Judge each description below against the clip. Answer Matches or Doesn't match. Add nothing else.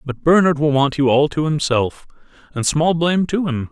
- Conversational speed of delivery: Doesn't match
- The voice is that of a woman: Doesn't match